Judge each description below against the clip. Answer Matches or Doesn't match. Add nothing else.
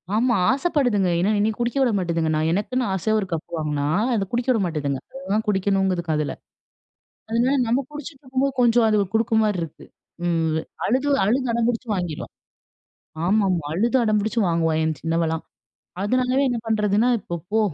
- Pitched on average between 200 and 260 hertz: Matches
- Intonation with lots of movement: Matches